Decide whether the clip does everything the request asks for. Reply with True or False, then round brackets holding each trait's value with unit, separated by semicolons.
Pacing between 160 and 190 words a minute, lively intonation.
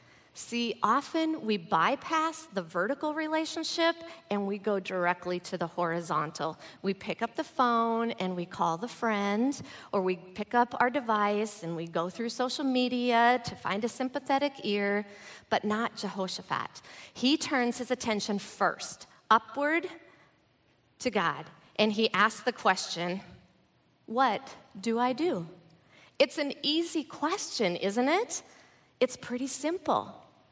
False (140 wpm; 6.1 semitones)